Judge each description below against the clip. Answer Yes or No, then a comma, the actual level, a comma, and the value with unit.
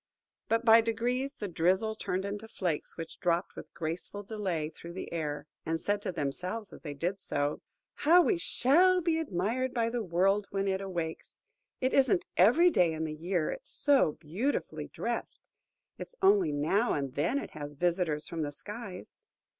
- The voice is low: No, high, 190 Hz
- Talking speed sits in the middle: Yes, average, 175 wpm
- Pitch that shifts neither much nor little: No, wide, 6.0 semitones